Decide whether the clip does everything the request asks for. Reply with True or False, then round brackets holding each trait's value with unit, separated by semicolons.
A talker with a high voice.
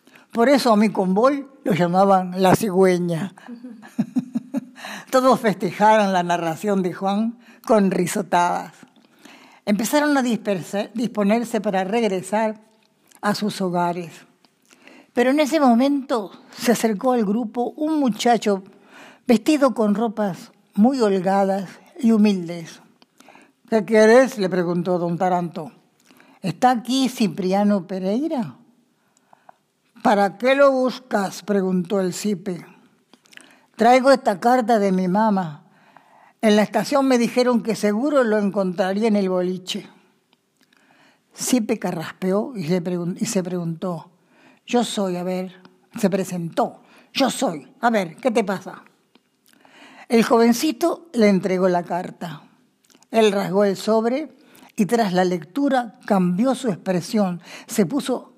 True (215 Hz)